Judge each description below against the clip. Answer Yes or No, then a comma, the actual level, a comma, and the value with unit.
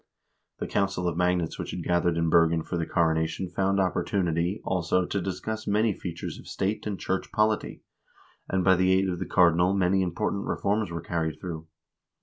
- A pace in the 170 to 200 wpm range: Yes, average, 185 wpm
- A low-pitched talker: Yes, very low, 90 Hz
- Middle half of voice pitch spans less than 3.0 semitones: Yes, narrow, 2.4 semitones